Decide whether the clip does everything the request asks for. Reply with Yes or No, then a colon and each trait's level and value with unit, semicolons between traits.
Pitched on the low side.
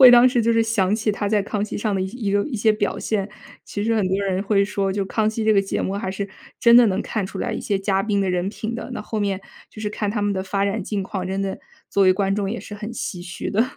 No: high, 205 Hz